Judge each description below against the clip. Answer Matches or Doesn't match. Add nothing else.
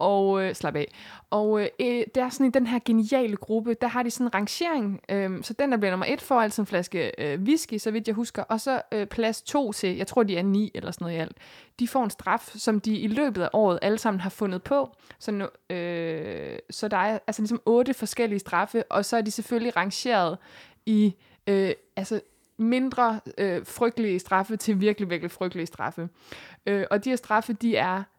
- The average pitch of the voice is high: Matches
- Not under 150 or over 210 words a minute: Doesn't match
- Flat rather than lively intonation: Doesn't match